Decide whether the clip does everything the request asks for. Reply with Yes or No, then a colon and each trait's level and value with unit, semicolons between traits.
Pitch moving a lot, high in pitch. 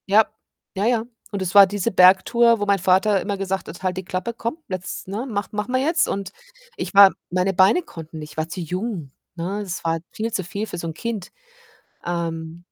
No: average, 3.3 semitones; high, 195 Hz